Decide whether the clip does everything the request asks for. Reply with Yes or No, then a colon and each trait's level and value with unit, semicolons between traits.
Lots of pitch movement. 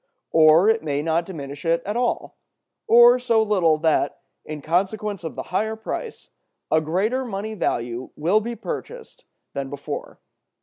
Yes: wide, 6.0 semitones